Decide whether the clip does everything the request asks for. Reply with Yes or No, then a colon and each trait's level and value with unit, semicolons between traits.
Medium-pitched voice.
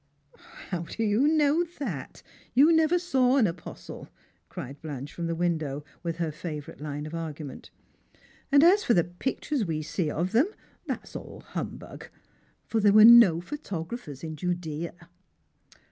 Yes: medium, 175 Hz